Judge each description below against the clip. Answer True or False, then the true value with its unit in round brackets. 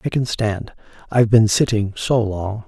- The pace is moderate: True (180 wpm)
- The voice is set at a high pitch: False (110 Hz)